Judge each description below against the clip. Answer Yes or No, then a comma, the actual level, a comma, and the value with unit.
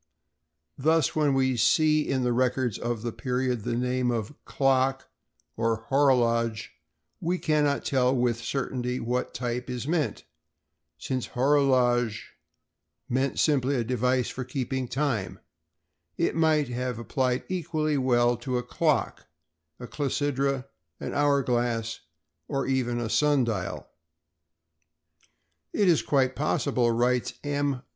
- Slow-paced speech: Yes, slow, 125 wpm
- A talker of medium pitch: No, low, 130 Hz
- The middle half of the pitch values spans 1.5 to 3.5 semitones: Yes, narrow, 2.6 semitones